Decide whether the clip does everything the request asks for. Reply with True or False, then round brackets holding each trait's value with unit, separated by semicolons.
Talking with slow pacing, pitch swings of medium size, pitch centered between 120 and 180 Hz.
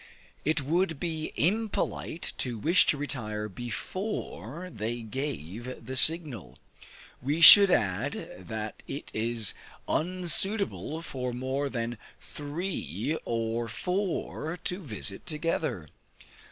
False (105 wpm; 6.5 semitones; 140 Hz)